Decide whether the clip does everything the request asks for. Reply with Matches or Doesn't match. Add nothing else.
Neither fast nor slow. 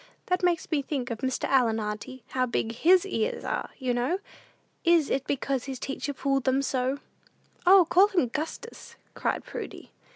Matches